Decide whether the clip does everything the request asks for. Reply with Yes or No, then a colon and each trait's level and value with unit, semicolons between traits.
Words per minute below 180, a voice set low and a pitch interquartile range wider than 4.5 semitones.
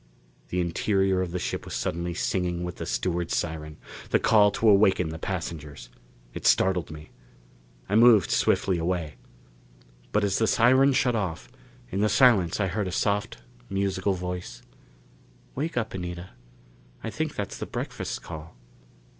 No: average, 155 wpm; very low, 90 Hz; average, 3.2 semitones